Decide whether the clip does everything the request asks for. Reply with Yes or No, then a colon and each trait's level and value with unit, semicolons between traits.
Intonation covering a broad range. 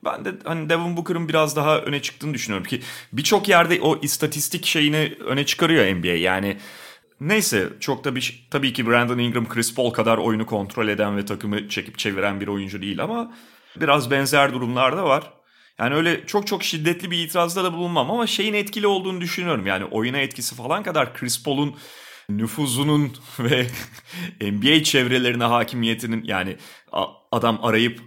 Yes: wide, 6.4 semitones